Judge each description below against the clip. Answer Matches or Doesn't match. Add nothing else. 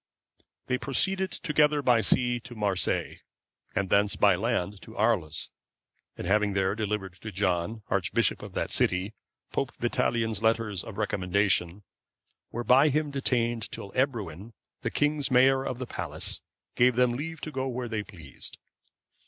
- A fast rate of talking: Doesn't match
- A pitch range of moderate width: Matches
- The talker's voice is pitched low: Matches